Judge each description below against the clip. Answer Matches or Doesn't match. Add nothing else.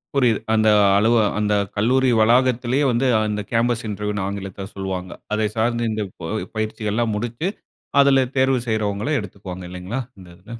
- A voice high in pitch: Doesn't match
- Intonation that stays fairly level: Doesn't match